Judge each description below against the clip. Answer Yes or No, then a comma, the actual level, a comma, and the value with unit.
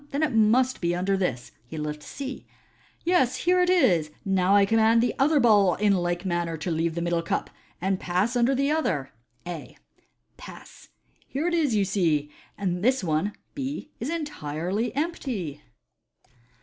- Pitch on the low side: No, high, 200 Hz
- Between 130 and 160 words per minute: No, average, 175 wpm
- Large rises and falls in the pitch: Yes, wide, 7.3 semitones